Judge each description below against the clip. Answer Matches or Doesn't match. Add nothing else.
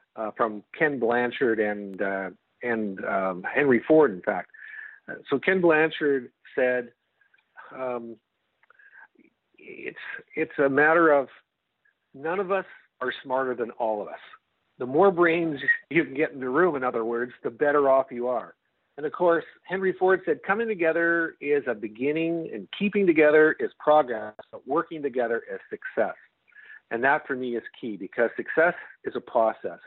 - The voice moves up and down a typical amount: Doesn't match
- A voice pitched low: Doesn't match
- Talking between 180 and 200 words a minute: Doesn't match